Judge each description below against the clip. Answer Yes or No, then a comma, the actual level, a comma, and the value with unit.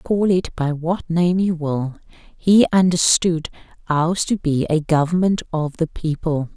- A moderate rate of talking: Yes, average, 155 wpm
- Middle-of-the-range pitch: Yes, medium, 165 Hz